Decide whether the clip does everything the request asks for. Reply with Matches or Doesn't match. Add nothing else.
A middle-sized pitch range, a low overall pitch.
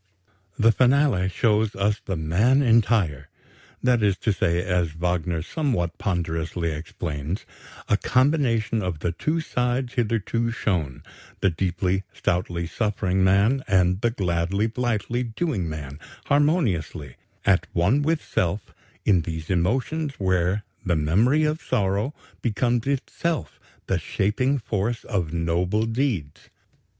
Doesn't match